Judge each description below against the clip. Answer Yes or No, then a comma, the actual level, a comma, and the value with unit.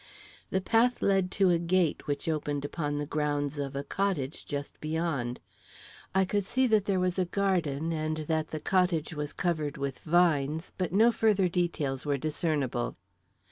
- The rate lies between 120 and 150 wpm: No, average, 170 wpm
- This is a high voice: No, medium, 160 Hz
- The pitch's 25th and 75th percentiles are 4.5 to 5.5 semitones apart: No, average, 4.1 semitones